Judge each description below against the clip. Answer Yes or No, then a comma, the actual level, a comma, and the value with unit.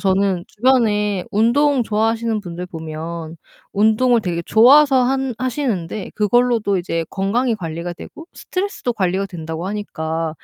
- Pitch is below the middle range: No, high, 210 Hz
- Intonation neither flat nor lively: No, wide, 5.7 semitones